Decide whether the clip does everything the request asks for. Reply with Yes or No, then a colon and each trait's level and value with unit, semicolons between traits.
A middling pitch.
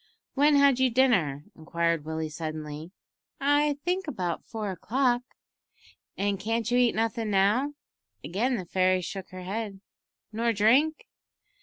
No: high, 215 Hz